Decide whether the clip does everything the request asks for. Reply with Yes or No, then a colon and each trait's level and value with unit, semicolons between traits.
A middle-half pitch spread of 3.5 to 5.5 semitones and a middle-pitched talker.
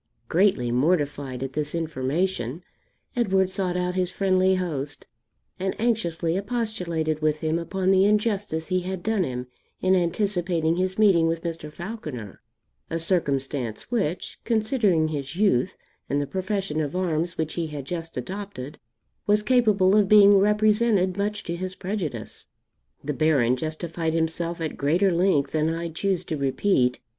Yes: average, 3.9 semitones; medium, 175 Hz